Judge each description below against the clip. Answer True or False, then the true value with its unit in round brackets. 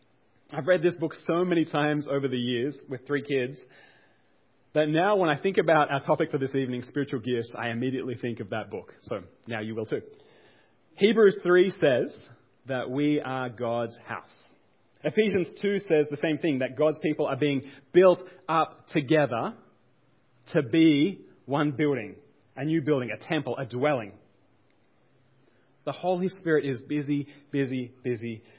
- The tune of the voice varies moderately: True (4.0 semitones)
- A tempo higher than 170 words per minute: False (160 wpm)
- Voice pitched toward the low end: False (145 Hz)